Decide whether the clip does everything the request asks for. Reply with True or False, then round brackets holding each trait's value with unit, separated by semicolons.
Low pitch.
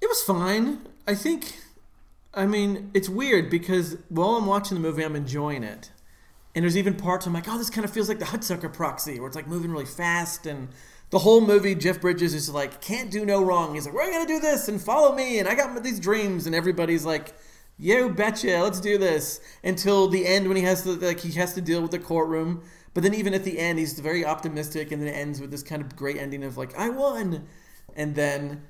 False (180 Hz)